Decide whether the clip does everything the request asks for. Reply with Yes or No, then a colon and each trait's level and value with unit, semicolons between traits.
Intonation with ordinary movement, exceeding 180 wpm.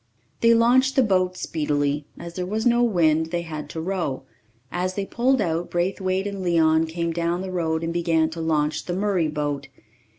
Yes: average, 3.1 semitones; average, 190 wpm